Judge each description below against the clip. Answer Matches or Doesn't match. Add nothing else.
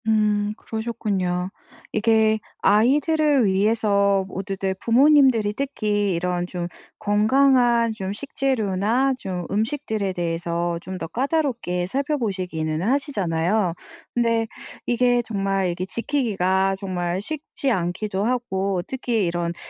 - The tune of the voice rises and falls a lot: Doesn't match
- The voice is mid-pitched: Doesn't match